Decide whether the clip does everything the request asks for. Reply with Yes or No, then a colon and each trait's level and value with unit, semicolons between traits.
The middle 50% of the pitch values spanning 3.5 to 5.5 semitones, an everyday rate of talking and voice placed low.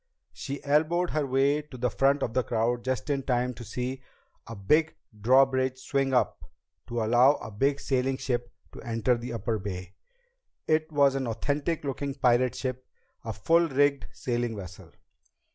No: average, 2.9 semitones; average, 165 wpm; low, 130 Hz